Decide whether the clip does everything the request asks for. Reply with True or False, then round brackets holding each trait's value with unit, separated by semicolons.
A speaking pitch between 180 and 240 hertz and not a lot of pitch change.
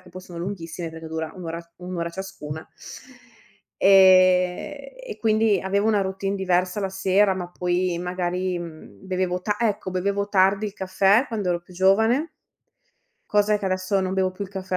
True (185 Hz; 1.9 semitones)